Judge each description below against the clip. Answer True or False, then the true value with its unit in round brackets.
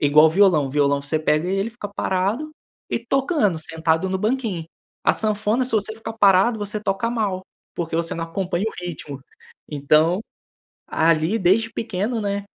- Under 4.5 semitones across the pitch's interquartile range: False (5.1 semitones)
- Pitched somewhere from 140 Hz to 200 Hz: True (190 Hz)